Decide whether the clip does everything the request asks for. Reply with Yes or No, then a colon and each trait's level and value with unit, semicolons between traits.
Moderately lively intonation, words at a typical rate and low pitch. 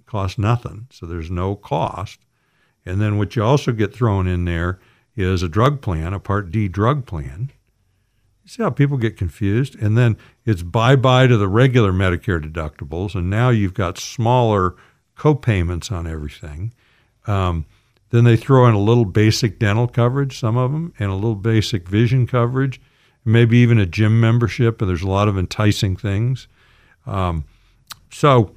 Yes: average, 4.2 semitones; average, 170 wpm; low, 110 Hz